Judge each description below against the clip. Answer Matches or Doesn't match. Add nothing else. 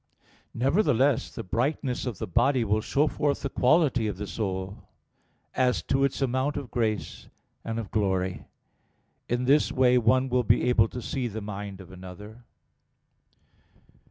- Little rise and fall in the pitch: Doesn't match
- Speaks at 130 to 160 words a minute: Matches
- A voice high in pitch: Doesn't match